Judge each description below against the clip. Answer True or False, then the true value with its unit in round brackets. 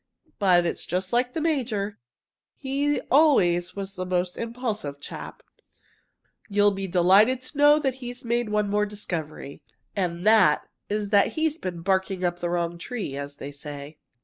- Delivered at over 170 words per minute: False (165 wpm)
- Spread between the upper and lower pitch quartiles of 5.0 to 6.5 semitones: True (5.6 semitones)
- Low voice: False (200 Hz)